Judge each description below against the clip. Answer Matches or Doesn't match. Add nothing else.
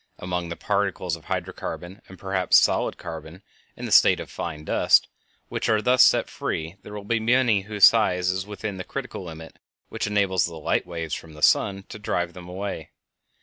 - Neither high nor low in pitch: Doesn't match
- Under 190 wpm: Doesn't match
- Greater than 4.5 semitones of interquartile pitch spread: Doesn't match